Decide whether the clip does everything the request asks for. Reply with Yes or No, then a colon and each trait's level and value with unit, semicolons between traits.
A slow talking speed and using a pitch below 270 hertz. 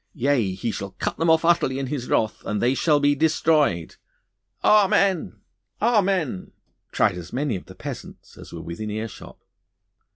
No: average, 160 wpm; low, 135 Hz